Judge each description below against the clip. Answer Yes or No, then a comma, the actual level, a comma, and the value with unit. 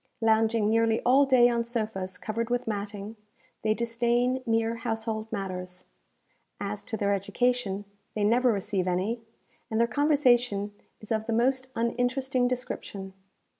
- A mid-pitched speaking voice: No, high, 225 Hz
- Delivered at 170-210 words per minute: No, slow, 135 wpm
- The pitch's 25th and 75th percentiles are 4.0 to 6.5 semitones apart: No, average, 2.9 semitones